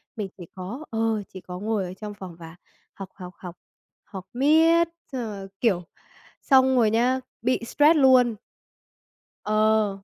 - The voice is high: Yes, high, 215 Hz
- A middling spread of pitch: Yes, average, 5.0 semitones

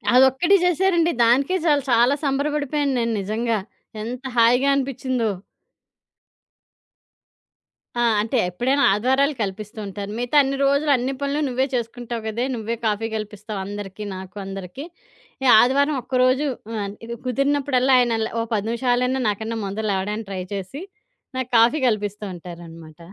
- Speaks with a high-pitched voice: Yes, high, 240 Hz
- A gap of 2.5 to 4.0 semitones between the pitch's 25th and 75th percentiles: No, average, 4.4 semitones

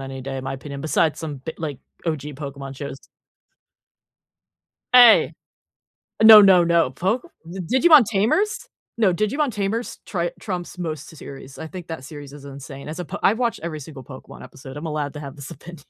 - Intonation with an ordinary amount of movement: No, wide, 6.0 semitones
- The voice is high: No, medium, 160 Hz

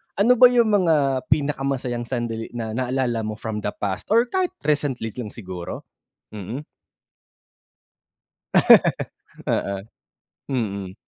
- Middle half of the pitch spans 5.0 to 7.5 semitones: Yes, wide, 5.5 semitones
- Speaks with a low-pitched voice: Yes, low, 125 Hz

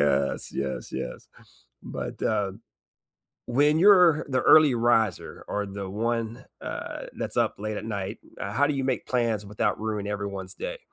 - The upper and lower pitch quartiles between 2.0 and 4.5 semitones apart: No, average, 4.9 semitones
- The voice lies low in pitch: Yes, low, 110 Hz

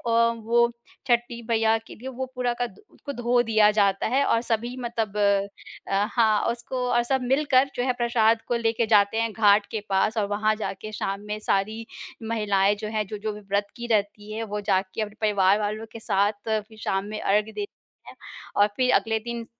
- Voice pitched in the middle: No, high, 220 Hz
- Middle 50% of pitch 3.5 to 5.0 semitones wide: No, narrow, 2.4 semitones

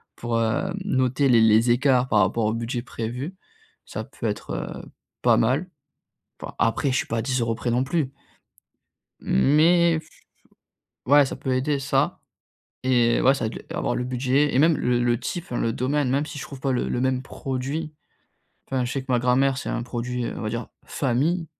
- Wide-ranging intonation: No, average, 2.9 semitones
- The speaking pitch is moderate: No, low, 130 Hz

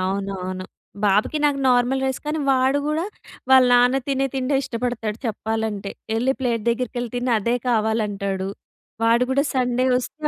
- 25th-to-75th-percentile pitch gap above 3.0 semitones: Yes, average, 3.6 semitones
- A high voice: Yes, high, 245 Hz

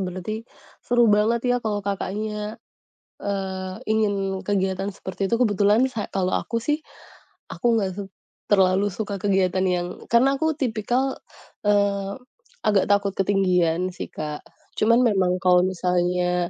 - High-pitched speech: Yes, high, 200 Hz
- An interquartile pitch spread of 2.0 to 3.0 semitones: Yes, average, 2.7 semitones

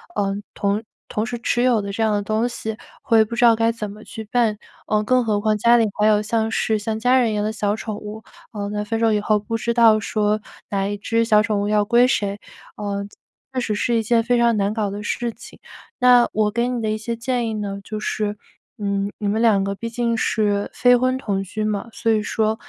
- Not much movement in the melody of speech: Yes, narrow, 1.9 semitones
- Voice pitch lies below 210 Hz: No, high, 215 Hz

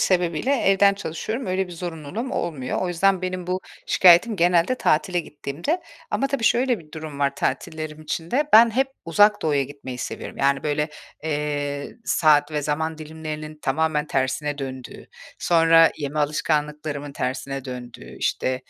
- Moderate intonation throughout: Yes, average, 4.0 semitones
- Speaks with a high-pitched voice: No, medium, 155 Hz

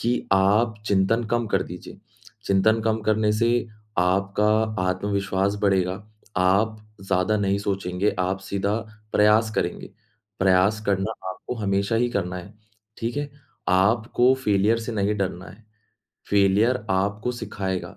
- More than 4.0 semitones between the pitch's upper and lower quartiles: No, narrow, 2.4 semitones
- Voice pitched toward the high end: No, low, 100 Hz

